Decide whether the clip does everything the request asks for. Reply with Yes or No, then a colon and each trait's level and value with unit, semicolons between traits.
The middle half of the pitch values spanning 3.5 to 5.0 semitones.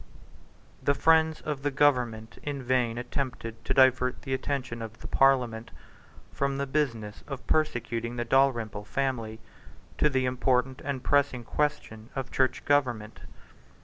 No: average, 2.9 semitones